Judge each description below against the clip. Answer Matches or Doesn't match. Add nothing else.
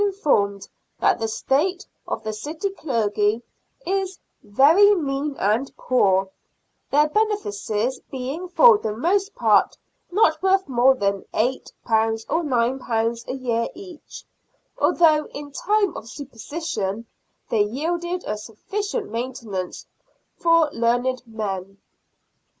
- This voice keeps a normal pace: Doesn't match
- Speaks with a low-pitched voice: Doesn't match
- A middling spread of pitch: Doesn't match